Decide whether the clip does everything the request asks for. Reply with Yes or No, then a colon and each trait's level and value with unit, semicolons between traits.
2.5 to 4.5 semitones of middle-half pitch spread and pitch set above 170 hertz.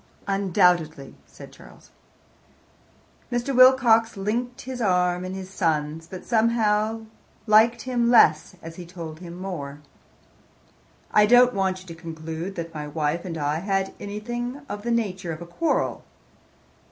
No: wide, 5.6 semitones; high, 190 Hz